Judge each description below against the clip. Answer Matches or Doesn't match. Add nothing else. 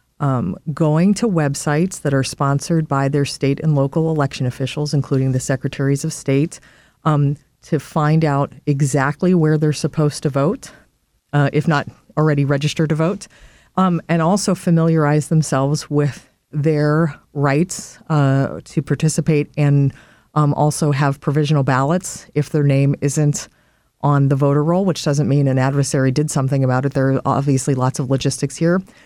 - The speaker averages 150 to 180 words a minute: Matches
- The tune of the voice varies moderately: Doesn't match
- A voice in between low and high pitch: Matches